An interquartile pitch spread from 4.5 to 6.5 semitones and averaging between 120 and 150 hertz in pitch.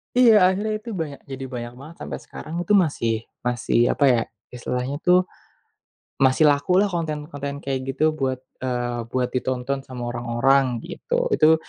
Yes: average, 4.9 semitones; medium, 140 Hz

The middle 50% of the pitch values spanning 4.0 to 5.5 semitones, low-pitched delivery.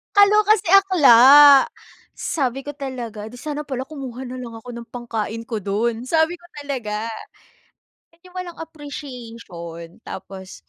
No: average, 4.8 semitones; very high, 255 Hz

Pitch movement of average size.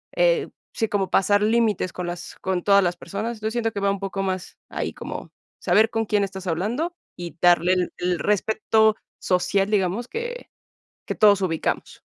Yes: average, 3.2 semitones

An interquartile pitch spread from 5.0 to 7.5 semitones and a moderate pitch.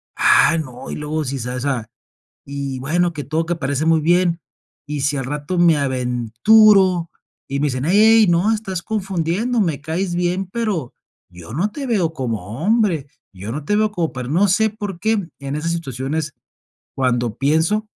Yes: average, 5.3 semitones; medium, 160 Hz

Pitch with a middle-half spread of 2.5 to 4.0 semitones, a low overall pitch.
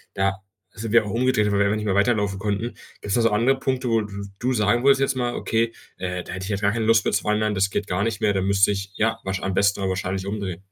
Yes: average, 2.8 semitones; low, 105 Hz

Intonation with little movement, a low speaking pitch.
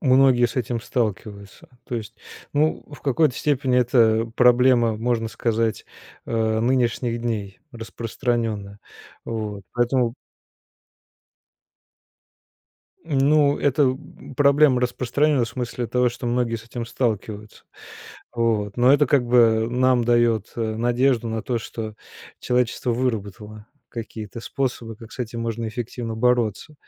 Yes: narrow, 2.1 semitones; low, 120 Hz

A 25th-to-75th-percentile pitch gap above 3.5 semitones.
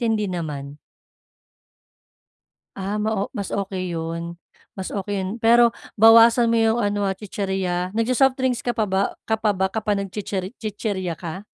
No: average, 3.1 semitones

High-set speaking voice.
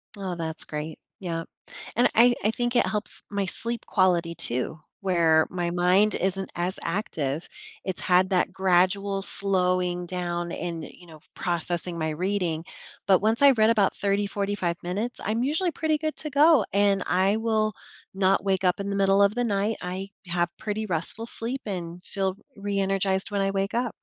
Yes: high, 195 Hz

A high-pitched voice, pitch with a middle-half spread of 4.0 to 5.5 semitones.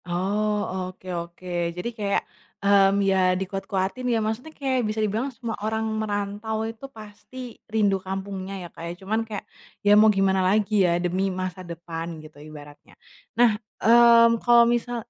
No: high, 205 Hz; average, 2.7 semitones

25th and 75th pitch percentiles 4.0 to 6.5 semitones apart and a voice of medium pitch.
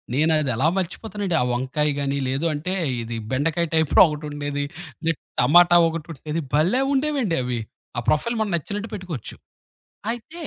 Yes: average, 4.6 semitones; medium, 160 Hz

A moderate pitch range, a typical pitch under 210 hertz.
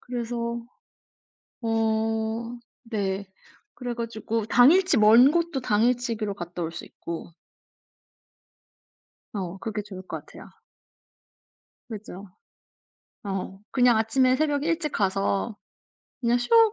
No: average, 3.3 semitones; high, 225 Hz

